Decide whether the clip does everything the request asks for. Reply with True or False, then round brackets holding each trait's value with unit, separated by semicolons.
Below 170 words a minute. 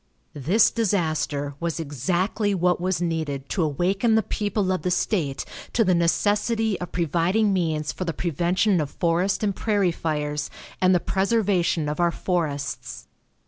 True (150 wpm)